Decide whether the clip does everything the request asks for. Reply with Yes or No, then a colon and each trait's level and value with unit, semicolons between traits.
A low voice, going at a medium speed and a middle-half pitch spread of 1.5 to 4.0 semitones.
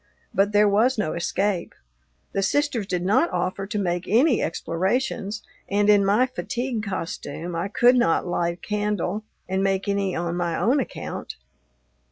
No: high, 200 Hz; average, 160 wpm; average, 3.5 semitones